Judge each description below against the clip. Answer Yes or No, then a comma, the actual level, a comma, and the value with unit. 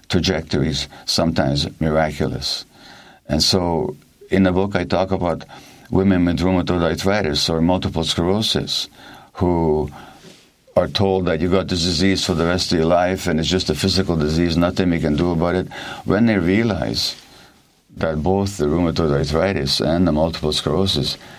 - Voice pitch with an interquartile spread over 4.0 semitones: No, average, 2.9 semitones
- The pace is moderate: Yes, average, 155 wpm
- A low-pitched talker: Yes, very low, 90 Hz